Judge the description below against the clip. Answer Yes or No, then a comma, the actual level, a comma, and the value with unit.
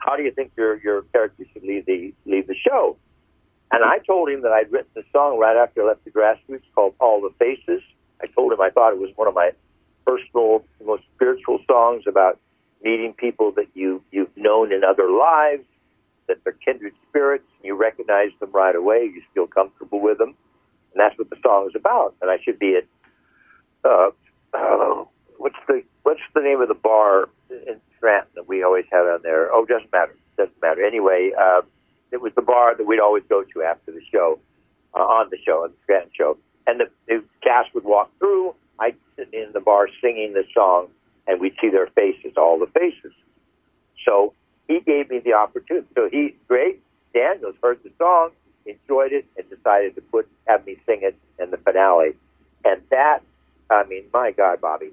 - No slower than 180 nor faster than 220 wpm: Yes, average, 200 wpm